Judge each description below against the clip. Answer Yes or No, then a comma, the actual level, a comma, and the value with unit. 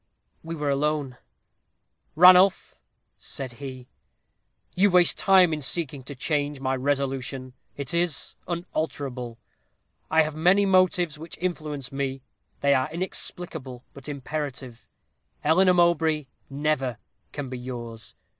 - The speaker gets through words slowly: Yes, slow, 115 wpm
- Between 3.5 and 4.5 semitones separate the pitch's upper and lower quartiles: Yes, average, 4.2 semitones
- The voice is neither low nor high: Yes, medium, 145 Hz